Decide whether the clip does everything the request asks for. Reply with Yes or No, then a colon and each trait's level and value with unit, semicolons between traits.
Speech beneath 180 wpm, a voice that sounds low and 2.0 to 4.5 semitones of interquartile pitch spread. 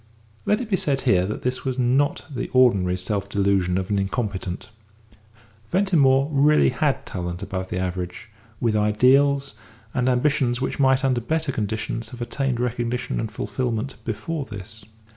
No: average, 155 wpm; low, 120 Hz; average, 5.0 semitones